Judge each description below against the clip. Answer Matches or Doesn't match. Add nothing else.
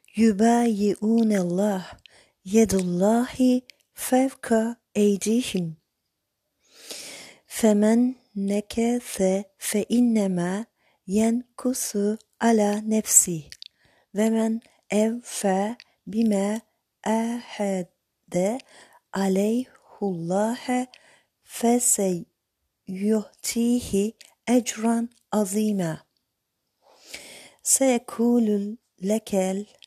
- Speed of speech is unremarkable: Doesn't match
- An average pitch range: Matches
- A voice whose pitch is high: Matches